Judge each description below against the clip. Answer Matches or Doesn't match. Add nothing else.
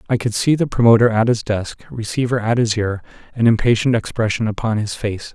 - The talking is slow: Doesn't match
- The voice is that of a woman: Doesn't match